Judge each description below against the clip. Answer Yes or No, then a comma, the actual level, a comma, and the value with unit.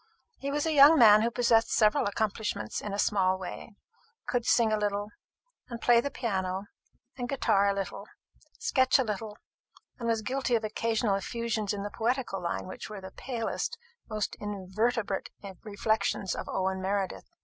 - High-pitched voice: Yes, high, 215 Hz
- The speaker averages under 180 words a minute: Yes, average, 165 wpm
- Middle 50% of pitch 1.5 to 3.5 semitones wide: Yes, average, 3.0 semitones